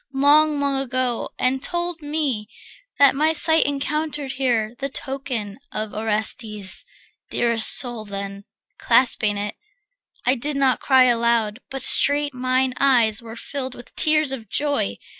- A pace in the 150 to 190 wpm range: No, average, 140 wpm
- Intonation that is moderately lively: Yes, average, 4.2 semitones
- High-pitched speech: Yes, very high, 255 Hz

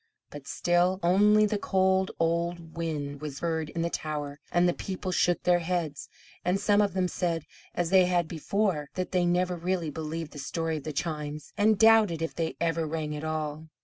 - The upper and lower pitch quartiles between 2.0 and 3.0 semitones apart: Yes, average, 2.7 semitones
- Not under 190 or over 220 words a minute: Yes, average, 195 wpm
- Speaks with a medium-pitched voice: Yes, medium, 170 Hz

